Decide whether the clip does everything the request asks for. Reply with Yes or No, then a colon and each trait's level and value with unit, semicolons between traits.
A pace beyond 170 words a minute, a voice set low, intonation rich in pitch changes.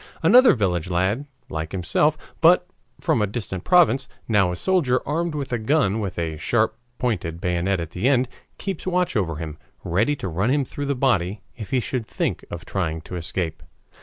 Yes: average, 190 wpm; low, 110 Hz; wide, 7.8 semitones